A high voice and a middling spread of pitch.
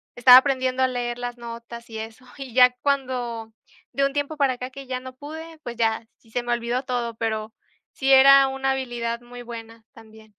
No: high, 245 Hz; narrow, 2.3 semitones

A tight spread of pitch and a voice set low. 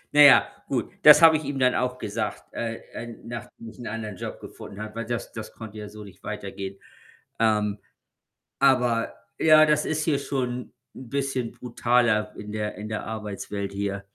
No: average, 3.3 semitones; low, 115 Hz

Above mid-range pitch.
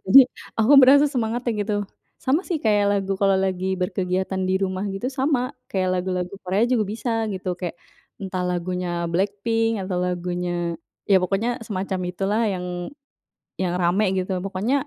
Yes: high, 195 Hz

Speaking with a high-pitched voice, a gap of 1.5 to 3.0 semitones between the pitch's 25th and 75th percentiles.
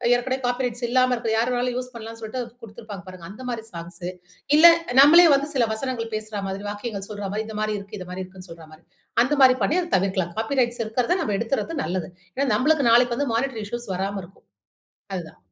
No: high, 225 Hz; average, 4.3 semitones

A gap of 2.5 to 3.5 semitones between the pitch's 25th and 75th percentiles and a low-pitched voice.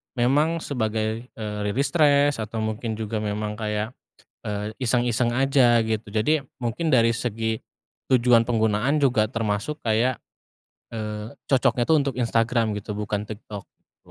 Yes: average, 2.9 semitones; low, 115 Hz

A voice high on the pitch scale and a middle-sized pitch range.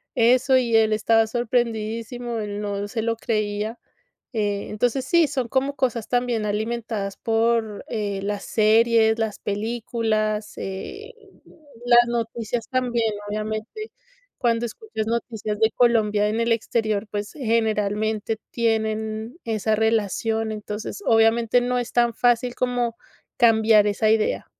No: high, 225 Hz; narrow, 1.8 semitones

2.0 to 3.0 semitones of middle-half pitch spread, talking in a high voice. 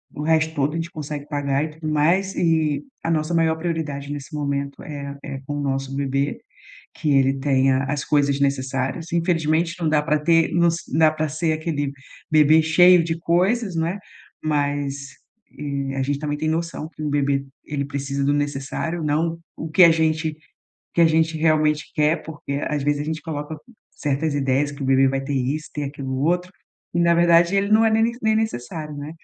No: narrow, 2.6 semitones; medium, 150 Hz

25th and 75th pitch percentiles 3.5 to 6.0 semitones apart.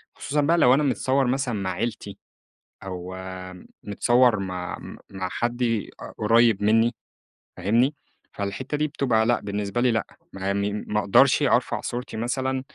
Yes: average, 4.1 semitones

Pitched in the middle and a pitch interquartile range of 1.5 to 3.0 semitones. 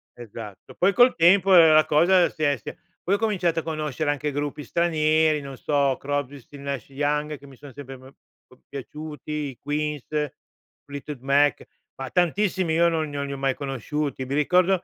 Yes: medium, 150 Hz; average, 2.7 semitones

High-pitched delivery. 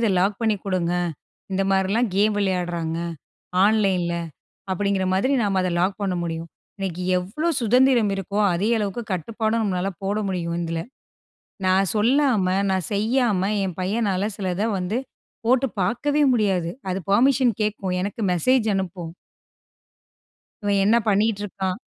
Yes: high, 195 Hz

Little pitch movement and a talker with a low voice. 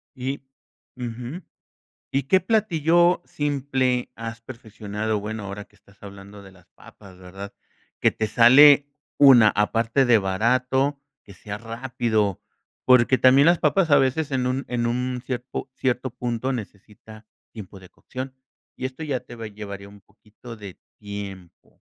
No: average, 4.2 semitones; low, 120 Hz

